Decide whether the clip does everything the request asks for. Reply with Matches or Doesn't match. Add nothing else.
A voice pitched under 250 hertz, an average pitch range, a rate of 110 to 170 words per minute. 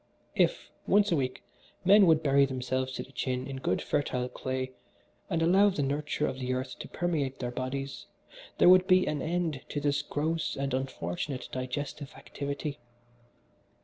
Matches